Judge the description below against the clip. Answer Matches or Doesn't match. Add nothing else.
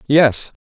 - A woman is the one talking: Doesn't match